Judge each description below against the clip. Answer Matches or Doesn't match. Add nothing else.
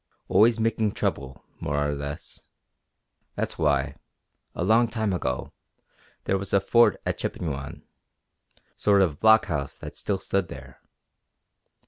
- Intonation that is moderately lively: Doesn't match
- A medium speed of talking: Doesn't match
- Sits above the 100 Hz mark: Doesn't match